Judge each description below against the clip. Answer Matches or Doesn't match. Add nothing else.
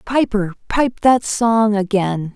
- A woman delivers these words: Matches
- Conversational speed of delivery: Doesn't match